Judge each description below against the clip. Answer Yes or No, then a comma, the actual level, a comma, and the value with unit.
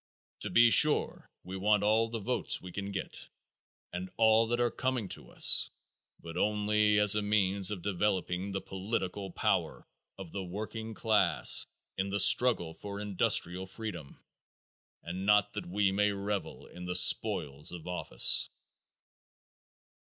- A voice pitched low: Yes, low, 100 Hz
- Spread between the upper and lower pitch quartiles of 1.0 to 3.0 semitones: Yes, narrow, 2.5 semitones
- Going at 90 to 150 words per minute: Yes, average, 145 wpm